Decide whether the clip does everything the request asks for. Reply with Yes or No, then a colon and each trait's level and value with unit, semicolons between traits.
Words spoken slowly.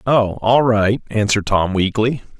Yes: slow, 125 wpm